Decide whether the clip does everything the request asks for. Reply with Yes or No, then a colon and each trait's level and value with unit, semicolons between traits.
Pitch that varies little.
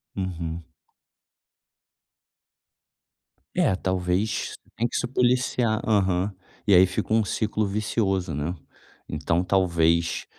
No: average, 3.4 semitones